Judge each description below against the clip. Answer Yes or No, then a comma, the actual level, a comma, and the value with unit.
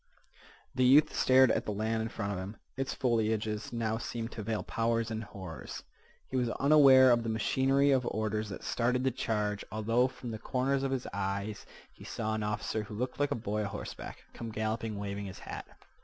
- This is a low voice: Yes, low, 110 Hz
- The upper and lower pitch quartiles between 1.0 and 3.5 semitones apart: Yes, average, 3.2 semitones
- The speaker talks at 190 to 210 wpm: Yes, average, 200 wpm